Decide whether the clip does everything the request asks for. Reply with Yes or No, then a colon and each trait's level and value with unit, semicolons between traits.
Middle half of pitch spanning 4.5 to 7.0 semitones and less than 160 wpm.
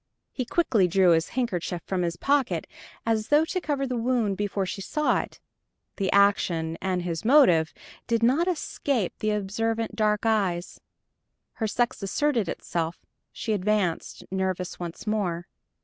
Yes: average, 4.8 semitones; average, 150 wpm